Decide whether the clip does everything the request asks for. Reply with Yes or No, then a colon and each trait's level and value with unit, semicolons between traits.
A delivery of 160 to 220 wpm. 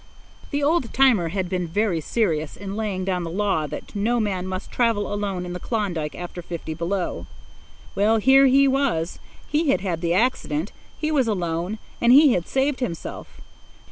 Yes: average, 175 wpm